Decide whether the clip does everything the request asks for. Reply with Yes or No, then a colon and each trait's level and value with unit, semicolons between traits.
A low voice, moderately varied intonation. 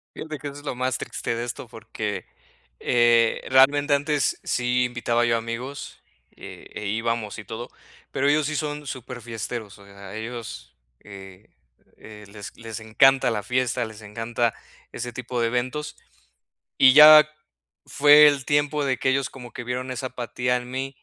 Yes: low, 125 Hz; average, 3.1 semitones